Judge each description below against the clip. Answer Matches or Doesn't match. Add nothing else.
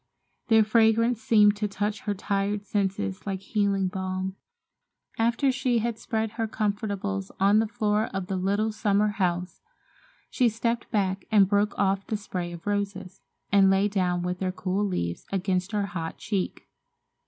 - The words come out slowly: Doesn't match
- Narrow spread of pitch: Matches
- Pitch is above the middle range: Matches